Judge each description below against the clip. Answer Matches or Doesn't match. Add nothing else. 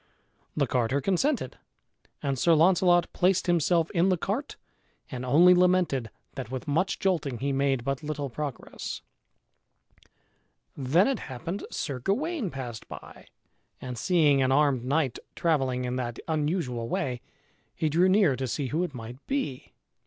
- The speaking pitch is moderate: Matches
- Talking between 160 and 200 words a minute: Doesn't match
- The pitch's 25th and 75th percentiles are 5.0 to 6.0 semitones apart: Matches